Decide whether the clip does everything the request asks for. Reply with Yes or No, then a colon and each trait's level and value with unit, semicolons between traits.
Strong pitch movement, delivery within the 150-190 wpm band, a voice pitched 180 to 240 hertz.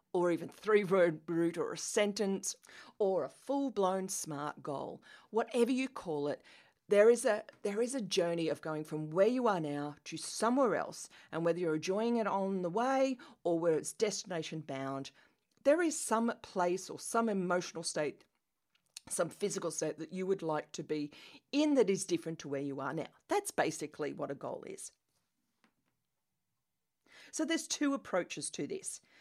Yes: wide, 6.3 semitones; average, 175 wpm; high, 190 Hz